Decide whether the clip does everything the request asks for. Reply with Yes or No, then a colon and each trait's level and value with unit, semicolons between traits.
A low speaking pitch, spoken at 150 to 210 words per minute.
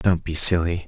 Yes: very low, 85 Hz; fast, 205 wpm